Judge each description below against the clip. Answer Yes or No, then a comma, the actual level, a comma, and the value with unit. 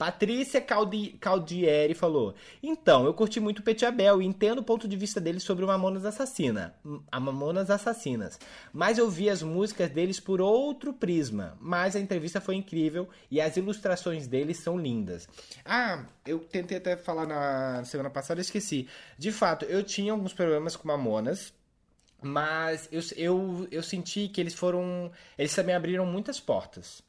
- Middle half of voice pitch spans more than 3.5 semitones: Yes, average, 4.2 semitones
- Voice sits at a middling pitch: Yes, medium, 180 Hz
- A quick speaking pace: No, average, 165 wpm